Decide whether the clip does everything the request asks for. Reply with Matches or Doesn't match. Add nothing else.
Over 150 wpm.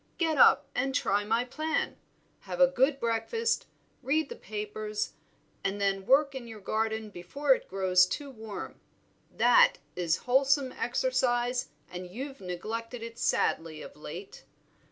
Doesn't match